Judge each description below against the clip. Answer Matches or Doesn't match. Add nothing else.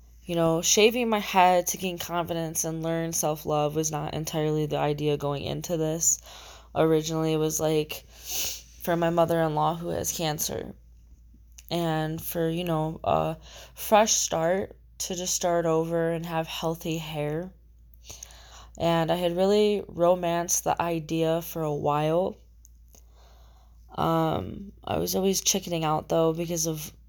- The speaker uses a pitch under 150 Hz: Doesn't match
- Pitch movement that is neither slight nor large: Doesn't match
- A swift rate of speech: Doesn't match